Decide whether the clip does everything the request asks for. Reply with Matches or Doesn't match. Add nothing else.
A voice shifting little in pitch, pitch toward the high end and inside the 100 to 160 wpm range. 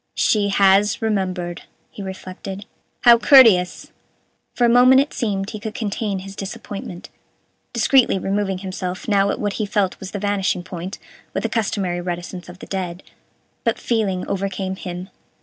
Matches